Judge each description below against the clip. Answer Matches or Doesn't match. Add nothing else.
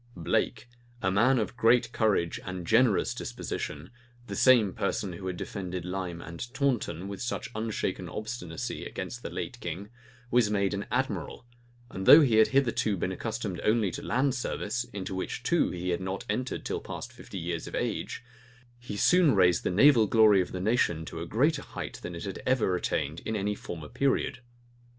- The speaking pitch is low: Matches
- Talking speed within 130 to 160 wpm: Doesn't match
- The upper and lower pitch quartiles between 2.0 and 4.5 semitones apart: Doesn't match